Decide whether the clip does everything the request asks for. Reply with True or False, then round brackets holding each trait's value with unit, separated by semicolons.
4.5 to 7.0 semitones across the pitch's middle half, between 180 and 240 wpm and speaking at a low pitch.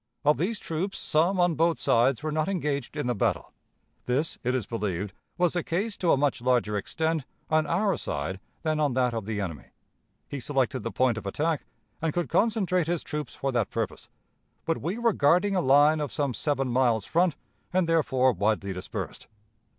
False (5.4 semitones; 190 wpm; 145 Hz)